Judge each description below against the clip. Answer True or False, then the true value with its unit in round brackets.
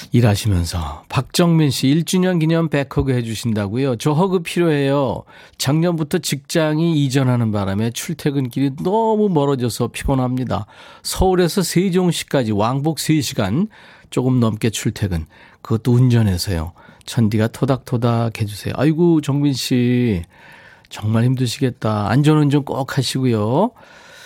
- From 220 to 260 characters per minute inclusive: False (295 characters per minute)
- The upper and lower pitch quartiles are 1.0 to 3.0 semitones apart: False (5.9 semitones)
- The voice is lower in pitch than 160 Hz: True (135 Hz)